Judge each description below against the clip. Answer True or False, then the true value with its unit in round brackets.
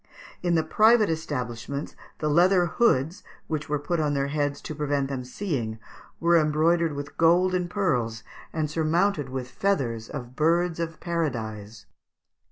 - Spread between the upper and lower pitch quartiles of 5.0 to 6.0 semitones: False (4.3 semitones)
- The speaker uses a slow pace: False (155 wpm)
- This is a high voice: False (155 Hz)